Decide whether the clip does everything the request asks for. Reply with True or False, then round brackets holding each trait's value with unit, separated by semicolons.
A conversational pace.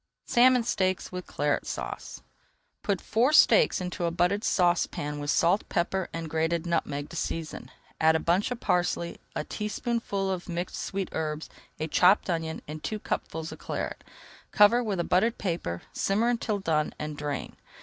True (165 wpm)